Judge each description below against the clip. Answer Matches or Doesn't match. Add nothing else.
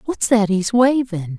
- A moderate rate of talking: Matches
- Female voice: Matches